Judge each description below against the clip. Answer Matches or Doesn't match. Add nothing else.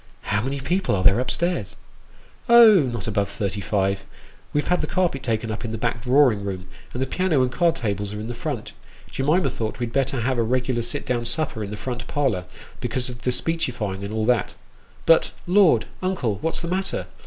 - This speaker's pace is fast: Matches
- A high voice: Doesn't match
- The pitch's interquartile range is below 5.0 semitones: Doesn't match